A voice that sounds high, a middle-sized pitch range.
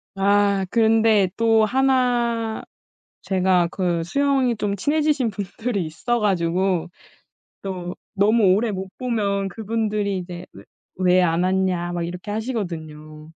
Yes: high, 200 Hz; average, 3.9 semitones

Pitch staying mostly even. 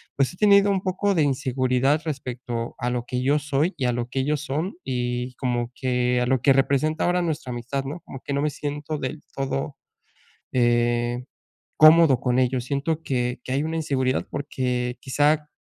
No: average, 3.3 semitones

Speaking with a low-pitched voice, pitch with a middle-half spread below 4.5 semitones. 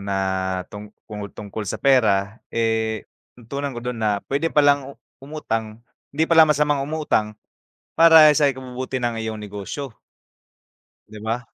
No: low, 120 Hz; average, 4.8 semitones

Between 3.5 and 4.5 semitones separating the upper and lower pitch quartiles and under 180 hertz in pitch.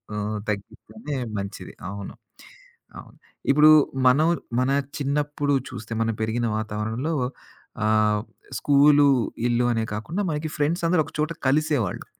No: wide, 5.5 semitones; low, 135 Hz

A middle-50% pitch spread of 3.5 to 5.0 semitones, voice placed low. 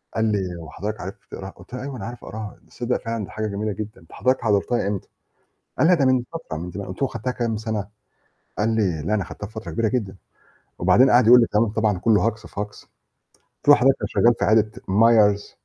No: average, 2.9 semitones; low, 110 Hz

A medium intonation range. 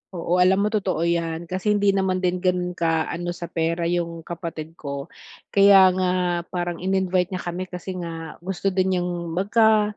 No: narrow, 2.0 semitones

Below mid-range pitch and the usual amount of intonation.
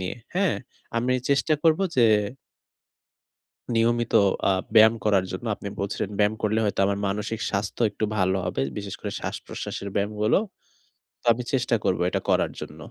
Yes: low, 105 Hz; average, 3.0 semitones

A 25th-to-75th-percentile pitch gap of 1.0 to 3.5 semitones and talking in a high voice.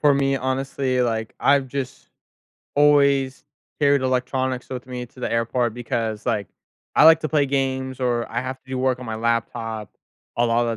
No: narrow, 2.5 semitones; low, 130 Hz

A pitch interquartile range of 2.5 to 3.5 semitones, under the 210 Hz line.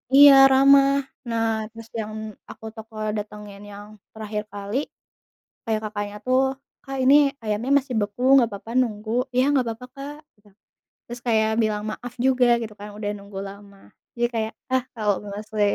No: average, 3.1 semitones; high, 220 Hz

